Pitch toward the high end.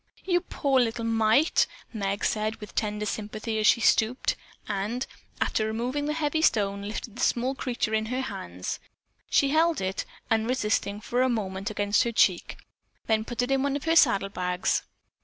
Yes: high, 225 Hz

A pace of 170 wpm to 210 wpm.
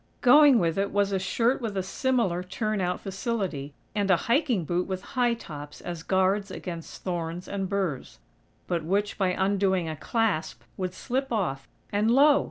Yes: average, 175 wpm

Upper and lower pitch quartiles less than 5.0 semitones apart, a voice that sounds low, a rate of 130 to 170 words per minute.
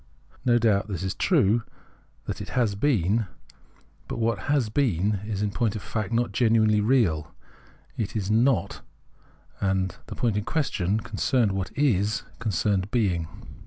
Yes: average, 3.3 semitones; low, 105 Hz; average, 150 wpm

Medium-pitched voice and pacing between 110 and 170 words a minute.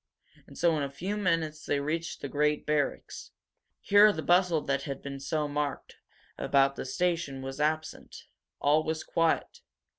Yes: medium, 150 Hz; average, 160 wpm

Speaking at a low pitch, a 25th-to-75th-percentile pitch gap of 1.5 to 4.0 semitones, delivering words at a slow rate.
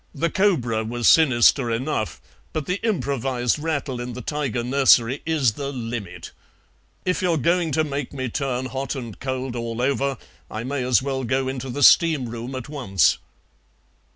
No: low, 130 Hz; average, 3.2 semitones; average, 165 wpm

